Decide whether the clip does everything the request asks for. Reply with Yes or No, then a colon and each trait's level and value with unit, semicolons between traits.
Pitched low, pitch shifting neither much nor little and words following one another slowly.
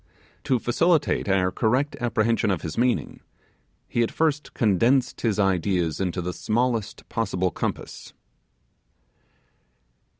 Yes: low, 110 Hz; average, 4.9 semitones; slow, 110 wpm